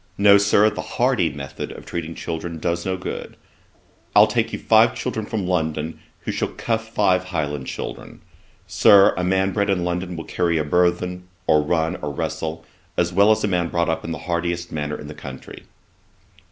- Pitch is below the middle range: Yes, very low, 85 Hz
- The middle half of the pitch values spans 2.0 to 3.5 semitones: Yes, average, 2.8 semitones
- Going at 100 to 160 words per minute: No, average, 190 wpm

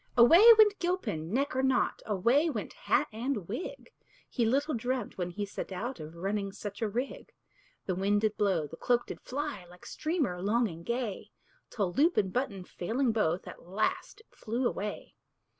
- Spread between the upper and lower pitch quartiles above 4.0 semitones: Yes, wide, 5.5 semitones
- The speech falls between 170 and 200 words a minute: Yes, average, 180 wpm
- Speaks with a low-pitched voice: No, high, 220 Hz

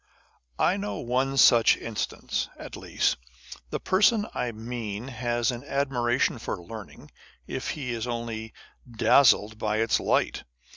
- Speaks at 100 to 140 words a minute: Yes, slow, 135 wpm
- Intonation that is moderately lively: No, narrow, 2.3 semitones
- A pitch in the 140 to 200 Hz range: No, low, 120 Hz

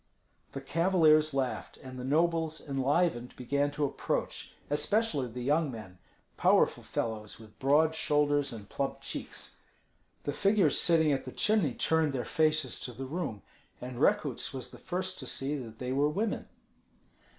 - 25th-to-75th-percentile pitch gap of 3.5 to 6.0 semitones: Yes, average, 4.0 semitones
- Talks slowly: No, average, 155 wpm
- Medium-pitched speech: Yes, medium, 145 Hz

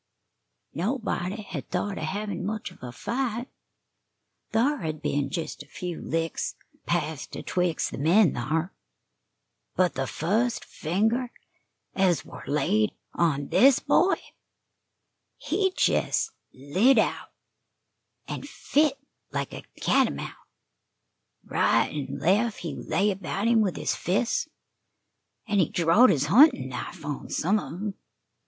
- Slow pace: Yes, slow, 125 wpm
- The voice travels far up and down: Yes, wide, 6.0 semitones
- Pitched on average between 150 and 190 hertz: Yes, medium, 185 Hz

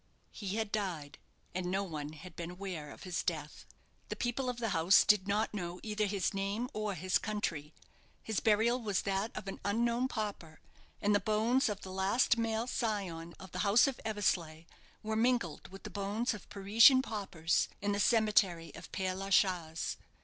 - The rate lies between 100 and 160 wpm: No, average, 185 wpm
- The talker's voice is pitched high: Yes, high, 200 Hz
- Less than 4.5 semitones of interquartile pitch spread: Yes, average, 3.3 semitones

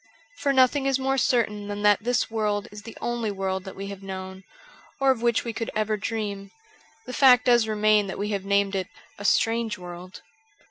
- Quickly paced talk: Yes, fast, 215 wpm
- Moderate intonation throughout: Yes, average, 3.2 semitones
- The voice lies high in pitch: Yes, high, 210 Hz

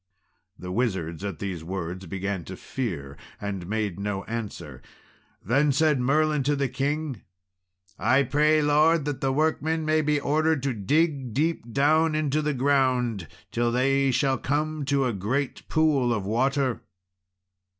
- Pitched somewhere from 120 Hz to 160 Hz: Yes, low, 135 Hz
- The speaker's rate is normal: Yes, average, 145 wpm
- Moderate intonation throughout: No, wide, 6.4 semitones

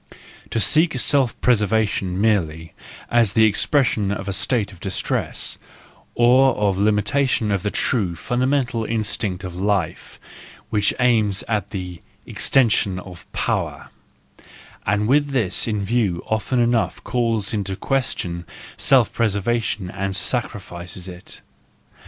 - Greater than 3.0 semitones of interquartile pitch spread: Yes, average, 3.7 semitones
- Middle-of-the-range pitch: No, low, 105 Hz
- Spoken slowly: Yes, slow, 120 wpm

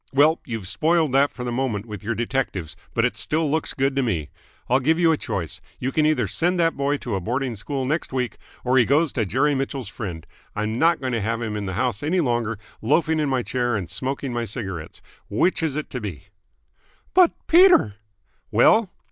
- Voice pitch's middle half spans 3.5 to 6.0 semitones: Yes, average, 5.2 semitones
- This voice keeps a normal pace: No, fast, 210 wpm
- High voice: No, low, 130 Hz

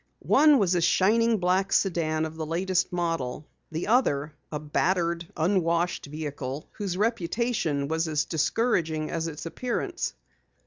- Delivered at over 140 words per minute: No, slow, 135 wpm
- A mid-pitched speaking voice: Yes, medium, 170 Hz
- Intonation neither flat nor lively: Yes, average, 3.8 semitones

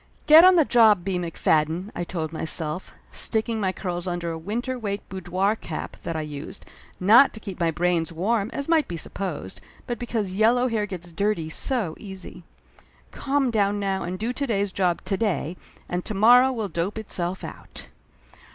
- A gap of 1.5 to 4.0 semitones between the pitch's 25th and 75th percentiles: No, average, 4.5 semitones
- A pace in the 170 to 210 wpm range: Yes, average, 190 wpm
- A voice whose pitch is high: Yes, high, 195 Hz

